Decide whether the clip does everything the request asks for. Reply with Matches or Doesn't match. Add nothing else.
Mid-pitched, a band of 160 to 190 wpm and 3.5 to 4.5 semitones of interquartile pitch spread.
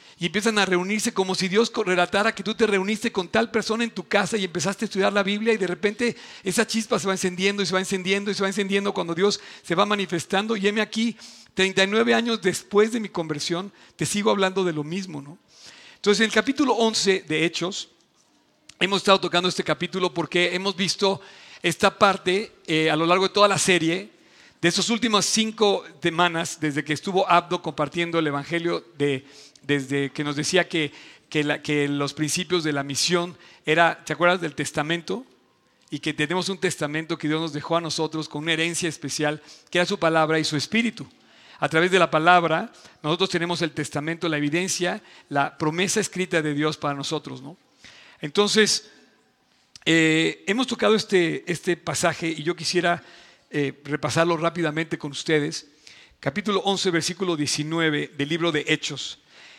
Matches